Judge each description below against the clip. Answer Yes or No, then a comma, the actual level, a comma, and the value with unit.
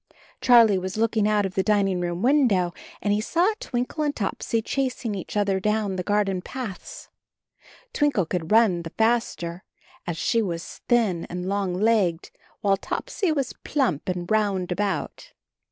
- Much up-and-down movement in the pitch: No, average, 4.1 semitones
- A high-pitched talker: Yes, high, 205 Hz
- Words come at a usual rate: Yes, average, 155 wpm